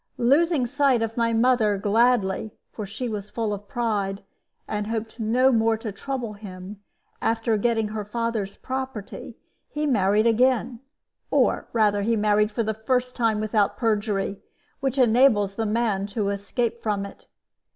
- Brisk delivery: No, average, 150 wpm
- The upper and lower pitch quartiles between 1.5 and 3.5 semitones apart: Yes, narrow, 2.6 semitones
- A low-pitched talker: No, high, 220 Hz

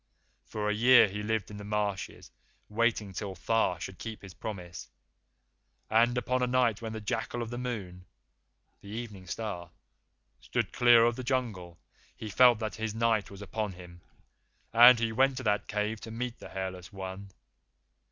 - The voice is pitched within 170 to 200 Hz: No, low, 110 Hz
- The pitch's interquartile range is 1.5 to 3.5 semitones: Yes, average, 3.2 semitones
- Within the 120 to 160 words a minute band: No, average, 170 wpm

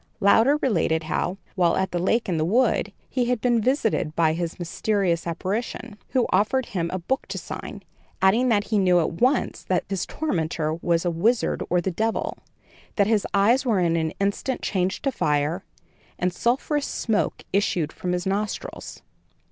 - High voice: Yes, high, 195 Hz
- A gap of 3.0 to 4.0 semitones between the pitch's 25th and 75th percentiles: No, average, 5.0 semitones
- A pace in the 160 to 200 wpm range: Yes, average, 175 wpm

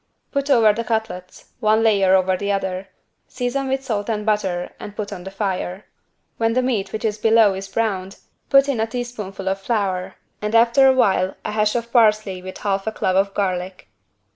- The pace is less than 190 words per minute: No, average, 195 wpm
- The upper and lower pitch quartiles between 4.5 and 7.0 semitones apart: No, average, 3.0 semitones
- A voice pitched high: Yes, high, 210 Hz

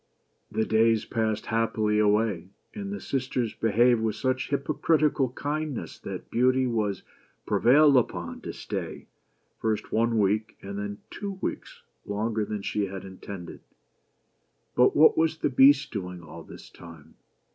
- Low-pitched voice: Yes, low, 115 Hz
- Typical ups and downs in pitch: Yes, average, 4.3 semitones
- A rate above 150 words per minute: No, average, 140 wpm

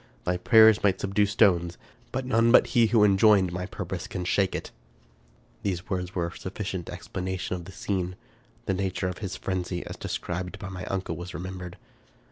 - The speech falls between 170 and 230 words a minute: Yes, average, 180 wpm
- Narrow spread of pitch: Yes, narrow, 2.2 semitones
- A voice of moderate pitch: No, very low, 95 Hz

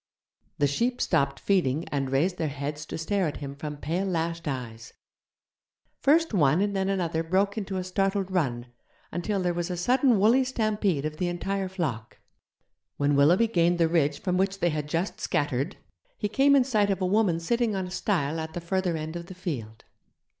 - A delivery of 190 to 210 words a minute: Yes, average, 195 wpm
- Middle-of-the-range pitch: Yes, medium, 175 Hz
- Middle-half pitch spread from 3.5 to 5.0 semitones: Yes, average, 4.7 semitones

